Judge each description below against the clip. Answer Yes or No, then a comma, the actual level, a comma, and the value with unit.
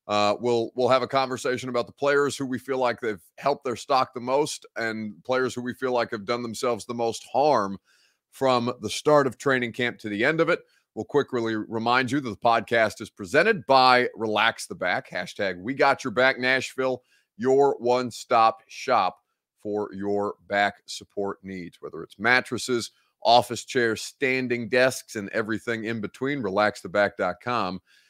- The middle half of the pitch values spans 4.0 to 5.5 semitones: No, average, 3.3 semitones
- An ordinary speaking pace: Yes, average, 175 wpm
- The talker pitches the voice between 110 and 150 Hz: Yes, low, 120 Hz